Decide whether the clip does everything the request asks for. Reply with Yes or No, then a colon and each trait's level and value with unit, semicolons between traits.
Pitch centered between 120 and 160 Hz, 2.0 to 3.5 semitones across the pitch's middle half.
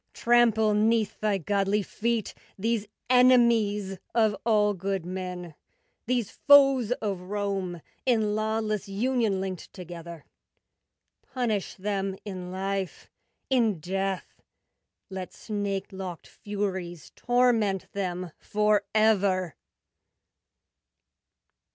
No: high, 205 Hz; average, 2.8 semitones